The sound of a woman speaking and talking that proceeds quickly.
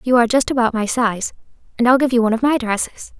Yes: female; fast, 265 wpm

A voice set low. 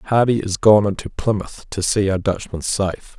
Yes: low, 100 Hz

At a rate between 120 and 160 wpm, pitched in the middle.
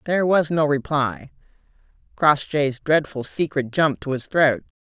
Yes: slow, 135 wpm; medium, 145 Hz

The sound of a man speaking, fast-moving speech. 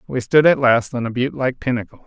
Yes: male; fast, 235 wpm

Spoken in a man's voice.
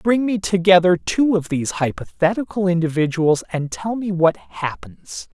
Yes: male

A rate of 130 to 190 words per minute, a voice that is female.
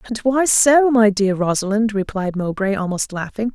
Yes: average, 170 wpm; female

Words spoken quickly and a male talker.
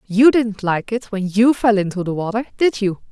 No: fast, 230 wpm; female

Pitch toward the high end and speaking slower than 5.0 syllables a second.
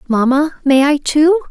Yes: very high, 295 Hz; 4.4 syllables/s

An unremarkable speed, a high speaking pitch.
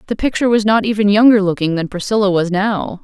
No: fast, 215 wpm; high, 205 Hz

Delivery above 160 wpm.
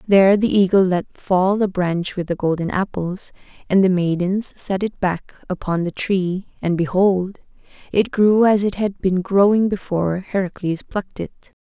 Yes: average, 170 wpm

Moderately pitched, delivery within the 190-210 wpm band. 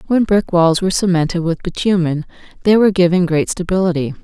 No: medium, 180 Hz; average, 170 wpm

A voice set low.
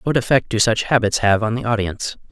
Yes: low, 115 Hz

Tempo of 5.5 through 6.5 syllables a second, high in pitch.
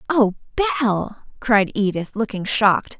Yes: 5.6 syllables/s; high, 220 Hz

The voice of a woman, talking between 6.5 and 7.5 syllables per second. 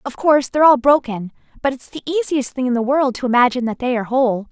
Yes: female; 6.9 syllables/s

